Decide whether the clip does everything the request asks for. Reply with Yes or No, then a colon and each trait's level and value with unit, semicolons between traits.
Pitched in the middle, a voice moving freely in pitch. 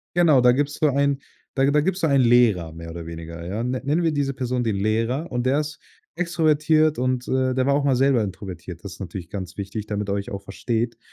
No: low, 125 Hz; wide, 6.2 semitones